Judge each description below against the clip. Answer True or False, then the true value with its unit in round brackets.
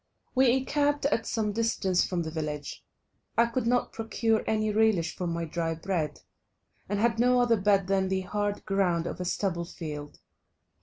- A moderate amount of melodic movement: True (4.9 semitones)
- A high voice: True (200 Hz)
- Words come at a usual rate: True (170 wpm)